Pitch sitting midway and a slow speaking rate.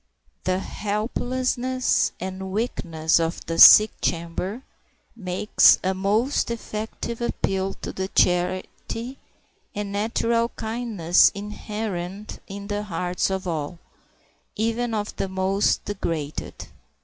No: high, 200 Hz; slow, 105 wpm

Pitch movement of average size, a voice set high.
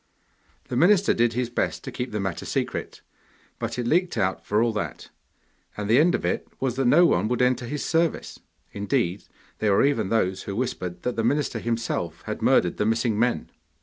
No: average, 4.0 semitones; low, 115 Hz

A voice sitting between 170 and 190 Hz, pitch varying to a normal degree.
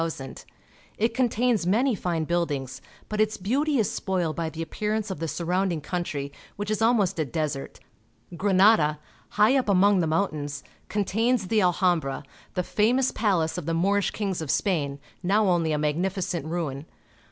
Yes: medium, 185 Hz; average, 4.7 semitones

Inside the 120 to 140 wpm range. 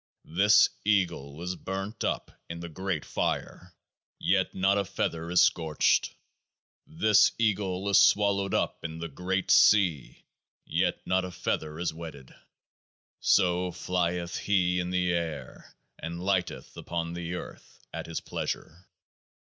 Yes: slow, 135 wpm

